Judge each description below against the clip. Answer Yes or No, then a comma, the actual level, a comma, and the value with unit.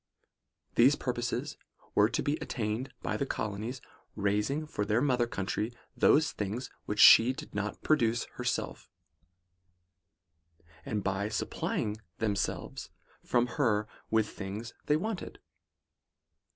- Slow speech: Yes, slow, 120 wpm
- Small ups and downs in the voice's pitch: No, average, 3.6 semitones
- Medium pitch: No, low, 110 Hz